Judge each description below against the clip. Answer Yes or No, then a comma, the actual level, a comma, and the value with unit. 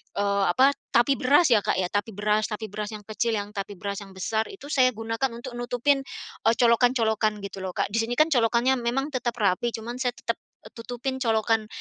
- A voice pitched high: Yes, high, 225 Hz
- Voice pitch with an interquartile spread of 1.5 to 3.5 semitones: Yes, average, 2.9 semitones